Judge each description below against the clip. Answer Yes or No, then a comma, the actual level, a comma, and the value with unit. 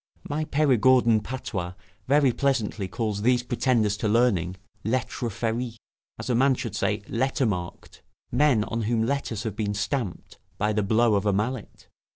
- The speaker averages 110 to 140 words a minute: No, average, 160 wpm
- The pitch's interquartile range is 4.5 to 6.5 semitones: No, average, 3.7 semitones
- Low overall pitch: Yes, low, 115 Hz